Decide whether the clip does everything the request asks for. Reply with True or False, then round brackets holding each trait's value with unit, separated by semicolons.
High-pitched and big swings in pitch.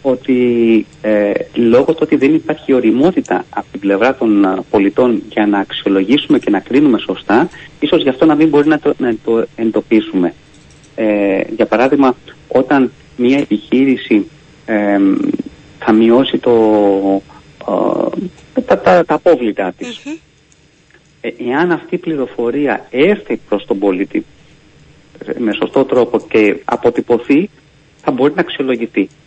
False (130 Hz; 5.7 semitones)